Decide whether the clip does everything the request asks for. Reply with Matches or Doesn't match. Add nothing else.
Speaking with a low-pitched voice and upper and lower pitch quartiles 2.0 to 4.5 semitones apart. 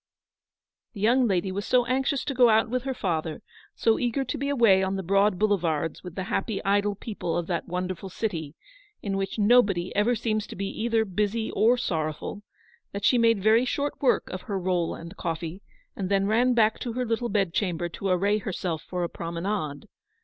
Doesn't match